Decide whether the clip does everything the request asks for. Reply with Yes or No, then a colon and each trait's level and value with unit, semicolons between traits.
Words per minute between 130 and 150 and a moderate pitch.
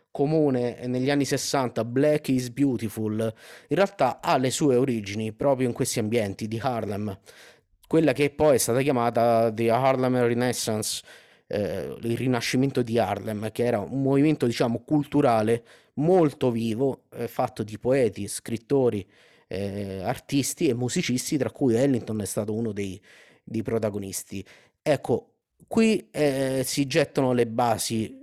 No: average, 140 wpm; low, 125 Hz